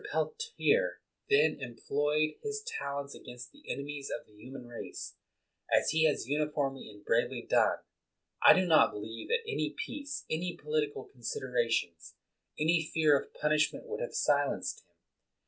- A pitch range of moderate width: No, wide, 6.2 semitones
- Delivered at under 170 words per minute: Yes, average, 150 wpm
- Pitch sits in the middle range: Yes, medium, 150 Hz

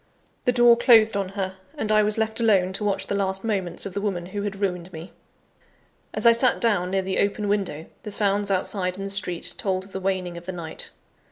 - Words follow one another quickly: Yes, fast, 230 wpm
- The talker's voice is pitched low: No, high, 195 Hz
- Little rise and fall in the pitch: Yes, narrow, 2.1 semitones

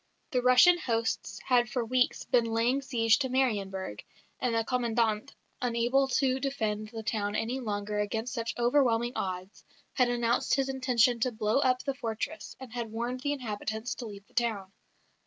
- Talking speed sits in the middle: Yes, average, 170 wpm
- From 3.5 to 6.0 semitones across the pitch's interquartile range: No, narrow, 2.6 semitones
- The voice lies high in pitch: Yes, high, 235 Hz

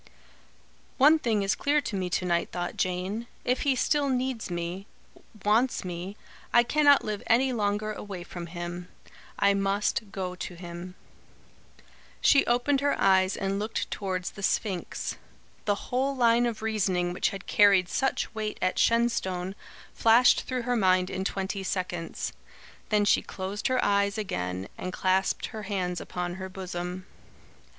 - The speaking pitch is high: Yes, high, 200 Hz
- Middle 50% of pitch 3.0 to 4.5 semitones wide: Yes, average, 4.2 semitones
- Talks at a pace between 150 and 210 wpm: Yes, average, 155 wpm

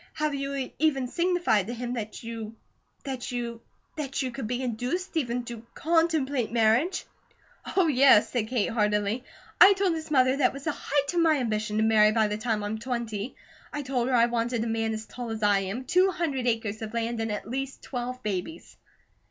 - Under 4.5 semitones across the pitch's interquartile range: Yes, average, 3.9 semitones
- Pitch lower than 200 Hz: No, high, 245 Hz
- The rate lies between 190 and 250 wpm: Yes, average, 200 wpm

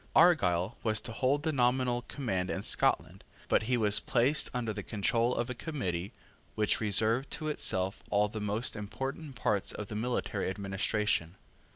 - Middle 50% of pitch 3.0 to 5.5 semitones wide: Yes, average, 3.8 semitones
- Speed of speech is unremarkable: Yes, average, 165 wpm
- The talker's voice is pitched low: Yes, low, 110 Hz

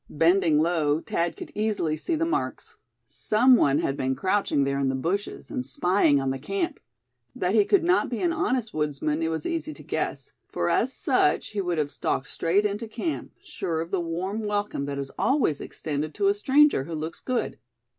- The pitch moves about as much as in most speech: No, wide, 6.4 semitones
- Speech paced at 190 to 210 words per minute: Yes, average, 200 wpm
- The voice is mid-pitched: Yes, medium, 175 Hz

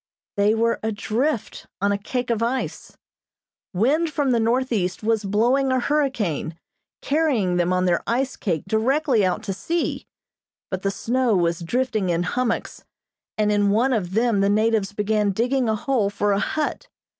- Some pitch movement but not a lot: Yes, average, 4.3 semitones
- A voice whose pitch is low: No, high, 220 Hz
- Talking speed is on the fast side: No, average, 165 wpm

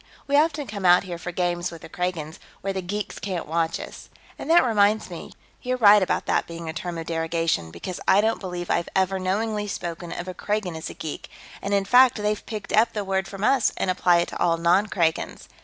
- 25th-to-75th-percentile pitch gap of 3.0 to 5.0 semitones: Yes, average, 3.5 semitones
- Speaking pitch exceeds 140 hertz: Yes, medium, 185 Hz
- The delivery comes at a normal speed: No, fast, 230 wpm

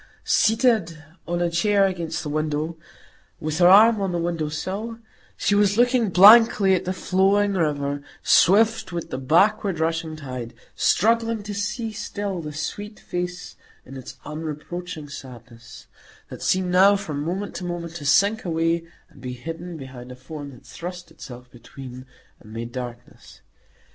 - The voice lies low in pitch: No, medium, 170 Hz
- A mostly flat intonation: No, average, 5.3 semitones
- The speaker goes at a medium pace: Yes, average, 155 wpm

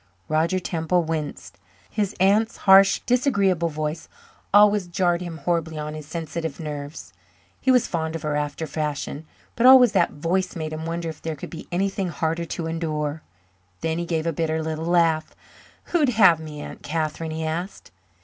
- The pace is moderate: Yes, average, 170 wpm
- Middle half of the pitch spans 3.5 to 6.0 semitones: No, average, 2.7 semitones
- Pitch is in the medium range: Yes, medium, 165 Hz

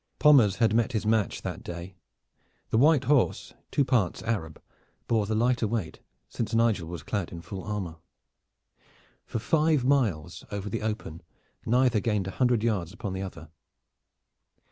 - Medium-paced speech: Yes, average, 155 wpm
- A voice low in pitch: Yes, low, 110 Hz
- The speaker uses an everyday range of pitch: Yes, average, 4.2 semitones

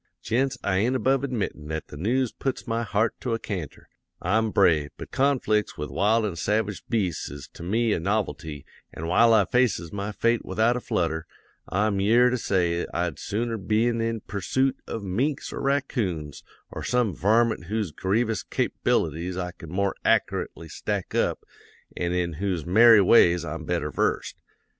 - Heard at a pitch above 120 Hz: No, low, 105 Hz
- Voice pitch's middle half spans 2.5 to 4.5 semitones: No, average, 5.0 semitones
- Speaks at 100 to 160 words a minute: No, average, 170 wpm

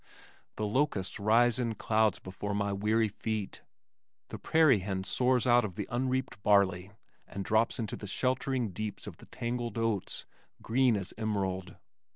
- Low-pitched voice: Yes, low, 110 Hz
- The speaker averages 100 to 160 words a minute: Yes, average, 155 wpm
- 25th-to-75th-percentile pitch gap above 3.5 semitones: No, average, 3.2 semitones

